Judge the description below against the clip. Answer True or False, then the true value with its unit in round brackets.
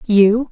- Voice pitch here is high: True (220 Hz)